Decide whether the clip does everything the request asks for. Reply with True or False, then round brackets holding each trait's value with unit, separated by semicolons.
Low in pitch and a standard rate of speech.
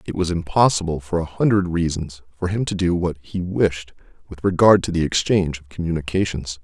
True (85 Hz; 190 wpm)